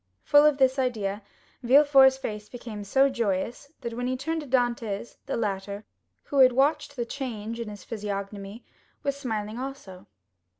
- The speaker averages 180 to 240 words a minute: No, average, 160 wpm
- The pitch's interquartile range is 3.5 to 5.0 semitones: Yes, average, 4.4 semitones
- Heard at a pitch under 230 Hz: No, high, 240 Hz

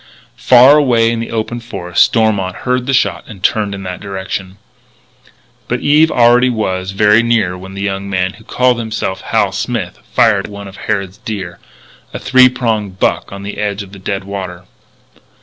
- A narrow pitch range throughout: No, average, 3.5 semitones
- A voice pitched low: Yes, low, 105 Hz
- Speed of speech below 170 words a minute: No, average, 185 wpm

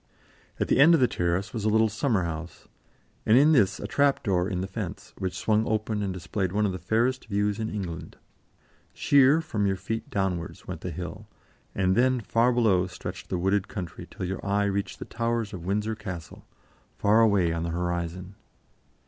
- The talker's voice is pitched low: Yes, low, 100 Hz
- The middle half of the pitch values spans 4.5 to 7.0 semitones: No, average, 3.5 semitones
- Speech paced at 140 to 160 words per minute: No, average, 195 wpm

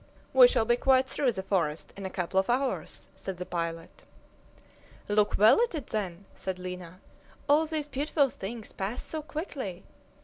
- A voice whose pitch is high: Yes, high, 210 Hz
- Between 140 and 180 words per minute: Yes, average, 170 wpm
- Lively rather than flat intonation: Yes, wide, 7.1 semitones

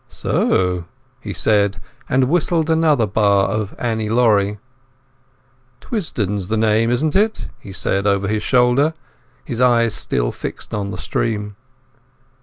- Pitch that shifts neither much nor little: Yes, average, 3.7 semitones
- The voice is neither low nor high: No, low, 110 Hz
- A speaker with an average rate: No, slow, 130 wpm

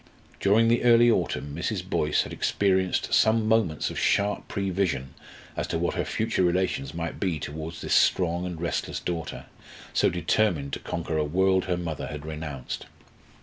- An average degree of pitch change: Yes, average, 4.0 semitones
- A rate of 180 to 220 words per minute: No, average, 165 wpm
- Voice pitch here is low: Yes, very low, 90 Hz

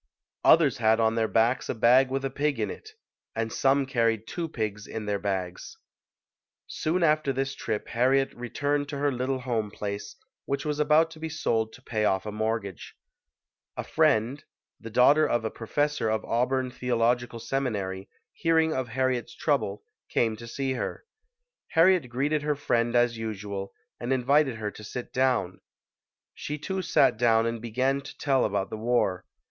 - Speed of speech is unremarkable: Yes, average, 170 wpm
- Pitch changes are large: No, average, 3.8 semitones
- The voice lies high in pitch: No, low, 120 Hz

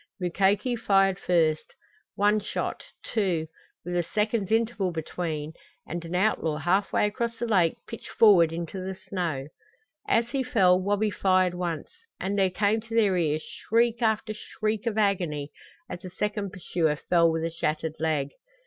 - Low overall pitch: No, medium, 185 Hz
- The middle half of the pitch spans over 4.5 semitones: No, average, 4.2 semitones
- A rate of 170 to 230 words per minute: No, average, 160 wpm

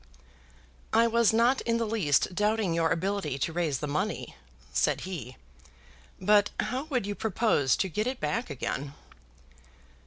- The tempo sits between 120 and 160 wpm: Yes, average, 150 wpm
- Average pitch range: No, wide, 6.2 semitones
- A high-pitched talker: Yes, high, 200 Hz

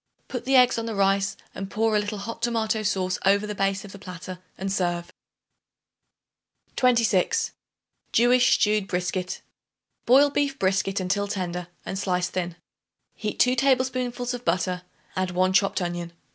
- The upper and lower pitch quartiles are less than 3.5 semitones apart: No, average, 4.1 semitones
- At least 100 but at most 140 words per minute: No, average, 155 wpm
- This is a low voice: No, high, 200 Hz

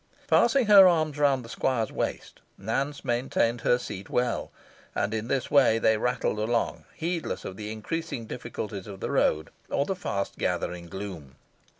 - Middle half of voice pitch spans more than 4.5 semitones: Yes, average, 5.3 semitones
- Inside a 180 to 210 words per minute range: No, average, 165 wpm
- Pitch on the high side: No, low, 120 Hz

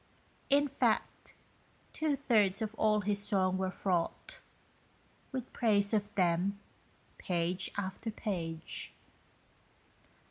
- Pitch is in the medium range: No, high, 200 Hz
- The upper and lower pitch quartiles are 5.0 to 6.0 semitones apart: No, average, 3.1 semitones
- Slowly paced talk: Yes, slow, 100 wpm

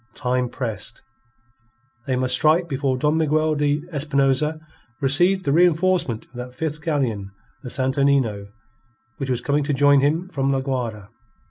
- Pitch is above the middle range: No, medium, 140 Hz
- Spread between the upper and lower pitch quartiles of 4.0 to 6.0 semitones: No, average, 3.1 semitones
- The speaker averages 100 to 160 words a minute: Yes, average, 150 wpm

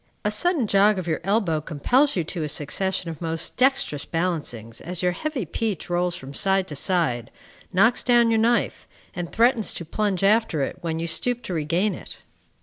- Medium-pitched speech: Yes, medium, 180 Hz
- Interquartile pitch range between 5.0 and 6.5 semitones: Yes, average, 5.3 semitones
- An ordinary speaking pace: Yes, average, 190 wpm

